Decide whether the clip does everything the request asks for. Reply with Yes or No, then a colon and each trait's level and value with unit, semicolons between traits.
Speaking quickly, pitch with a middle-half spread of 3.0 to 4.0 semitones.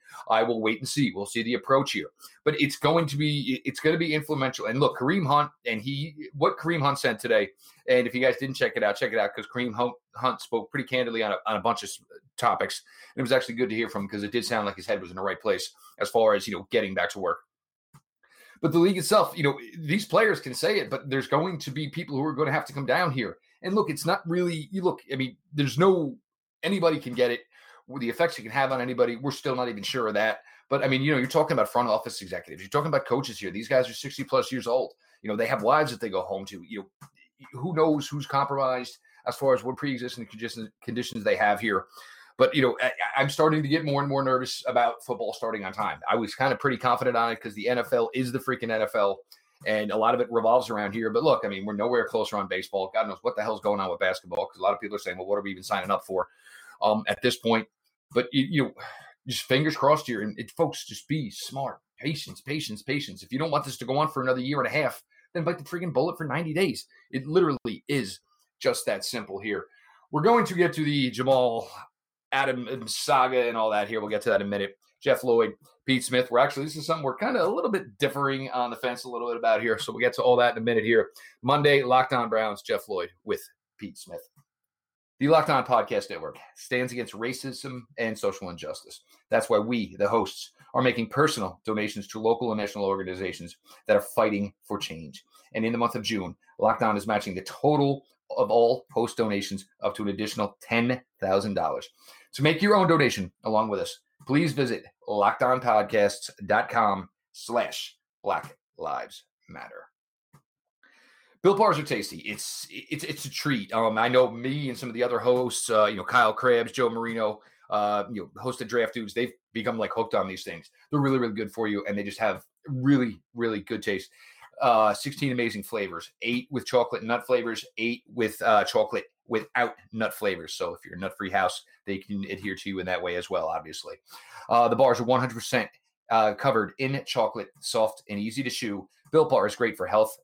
No: fast, 235 wpm; average, 4.9 semitones